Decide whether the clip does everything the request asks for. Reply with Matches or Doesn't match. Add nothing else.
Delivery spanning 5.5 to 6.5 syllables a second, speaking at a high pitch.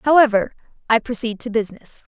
Matches